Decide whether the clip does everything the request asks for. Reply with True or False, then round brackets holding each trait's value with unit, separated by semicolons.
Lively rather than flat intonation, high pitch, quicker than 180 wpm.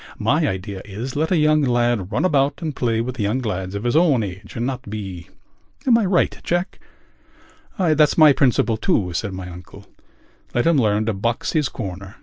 False (6.8 semitones; 120 Hz; 190 wpm)